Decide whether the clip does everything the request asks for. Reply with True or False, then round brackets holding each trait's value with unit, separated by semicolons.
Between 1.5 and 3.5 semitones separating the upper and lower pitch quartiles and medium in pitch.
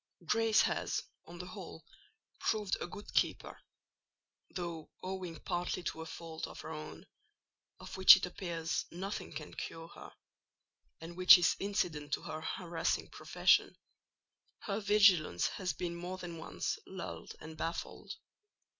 True (2.6 semitones; 175 Hz)